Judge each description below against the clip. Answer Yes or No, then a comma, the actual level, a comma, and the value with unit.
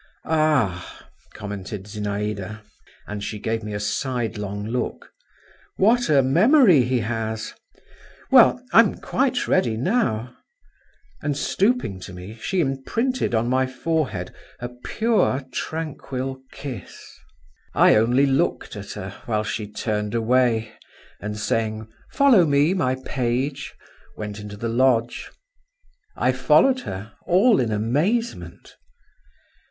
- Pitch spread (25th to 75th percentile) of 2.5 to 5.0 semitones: No, wide, 5.6 semitones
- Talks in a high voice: No, low, 120 Hz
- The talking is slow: Yes, slow, 115 wpm